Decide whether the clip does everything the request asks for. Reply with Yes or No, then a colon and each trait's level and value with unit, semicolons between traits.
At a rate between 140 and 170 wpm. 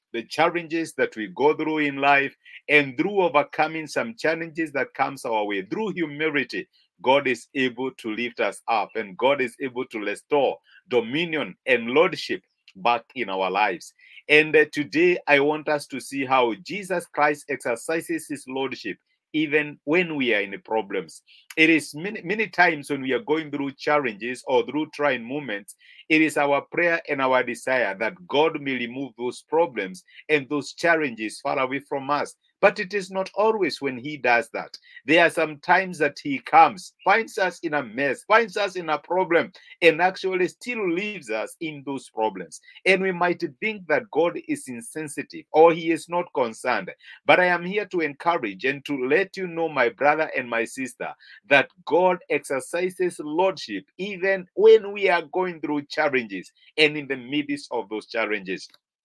No: average, 180 wpm